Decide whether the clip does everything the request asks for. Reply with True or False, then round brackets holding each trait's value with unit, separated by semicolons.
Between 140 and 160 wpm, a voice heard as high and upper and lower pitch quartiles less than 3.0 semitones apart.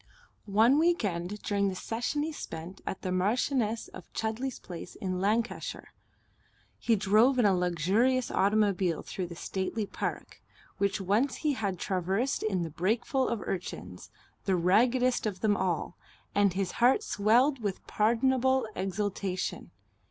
False (145 wpm; 205 Hz; 4.5 semitones)